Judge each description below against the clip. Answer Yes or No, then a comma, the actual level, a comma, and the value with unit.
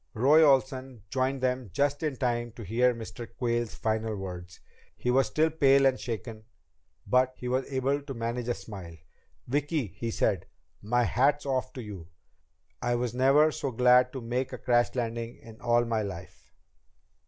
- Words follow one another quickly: No, average, 170 wpm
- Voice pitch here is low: Yes, low, 125 Hz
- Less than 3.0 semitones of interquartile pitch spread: Yes, narrow, 2.6 semitones